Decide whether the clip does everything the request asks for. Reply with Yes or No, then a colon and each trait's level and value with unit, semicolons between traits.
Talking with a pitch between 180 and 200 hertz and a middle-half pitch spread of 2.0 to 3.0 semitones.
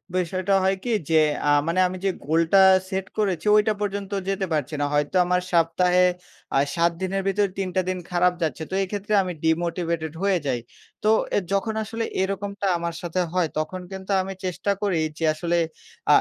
Yes: medium, 185 Hz; average, 2.7 semitones